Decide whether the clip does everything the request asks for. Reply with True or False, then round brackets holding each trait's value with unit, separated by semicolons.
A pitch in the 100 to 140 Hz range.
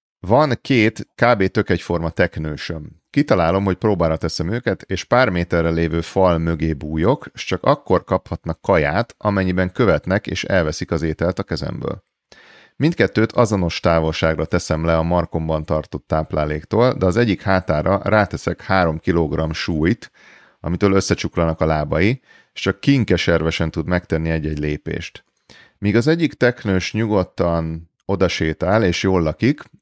False (85 Hz)